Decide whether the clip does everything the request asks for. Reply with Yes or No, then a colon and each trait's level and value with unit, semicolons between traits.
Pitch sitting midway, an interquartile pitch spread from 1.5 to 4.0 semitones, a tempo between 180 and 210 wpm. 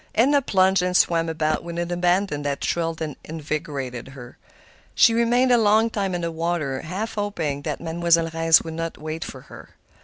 Yes: medium, 165 Hz; average, 3.6 semitones; average, 185 wpm